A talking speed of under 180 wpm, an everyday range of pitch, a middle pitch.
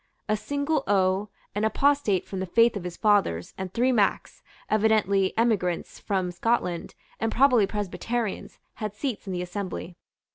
No: average, 150 wpm; average, 3.5 semitones; high, 205 Hz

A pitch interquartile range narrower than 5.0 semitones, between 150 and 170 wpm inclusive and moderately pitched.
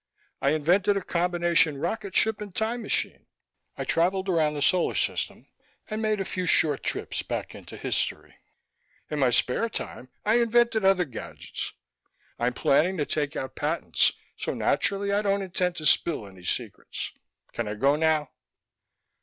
No: wide, 5.5 semitones; average, 160 wpm; medium, 175 Hz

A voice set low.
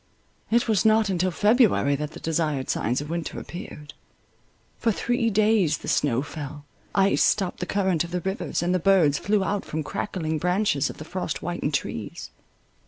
No: medium, 180 Hz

